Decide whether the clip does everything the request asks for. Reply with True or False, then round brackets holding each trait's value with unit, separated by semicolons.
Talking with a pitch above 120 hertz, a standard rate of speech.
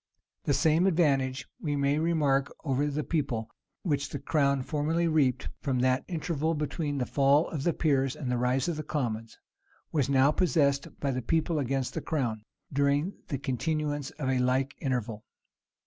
True (140 Hz; 165 wpm)